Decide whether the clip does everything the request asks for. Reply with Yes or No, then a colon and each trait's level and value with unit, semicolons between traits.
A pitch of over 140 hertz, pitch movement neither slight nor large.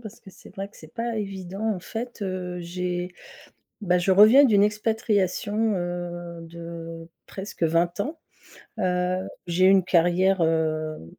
Yes: medium, 185 Hz; average, 3.0 semitones